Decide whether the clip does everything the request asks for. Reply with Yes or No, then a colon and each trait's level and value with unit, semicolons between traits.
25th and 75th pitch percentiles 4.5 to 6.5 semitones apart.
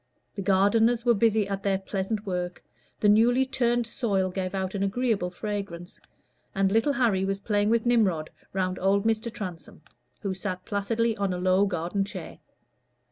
No: average, 3.1 semitones